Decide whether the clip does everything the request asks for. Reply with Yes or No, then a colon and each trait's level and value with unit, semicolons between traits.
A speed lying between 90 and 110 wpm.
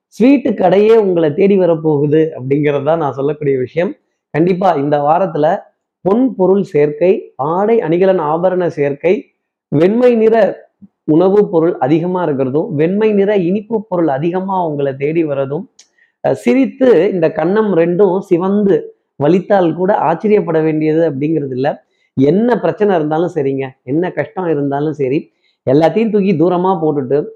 No: average, 125 wpm